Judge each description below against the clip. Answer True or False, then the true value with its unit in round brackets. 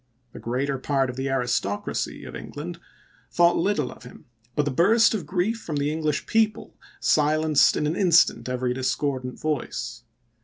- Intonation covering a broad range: False (4.8 semitones)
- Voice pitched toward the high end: False (145 Hz)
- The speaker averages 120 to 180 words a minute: True (160 wpm)